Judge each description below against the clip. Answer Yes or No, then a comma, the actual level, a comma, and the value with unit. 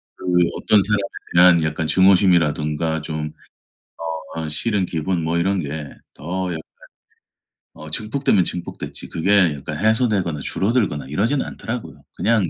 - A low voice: Yes, very low, 90 Hz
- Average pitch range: Yes, average, 4.7 semitones